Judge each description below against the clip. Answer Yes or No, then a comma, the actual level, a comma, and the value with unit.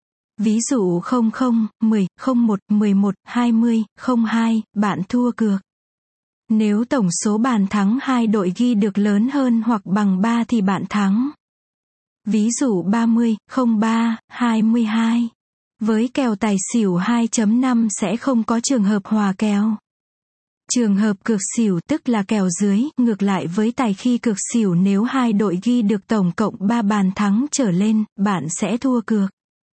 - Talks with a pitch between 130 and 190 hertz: No, high, 220 Hz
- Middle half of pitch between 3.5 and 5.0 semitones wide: No, narrow, 2.4 semitones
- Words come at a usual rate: No, slow, 155 wpm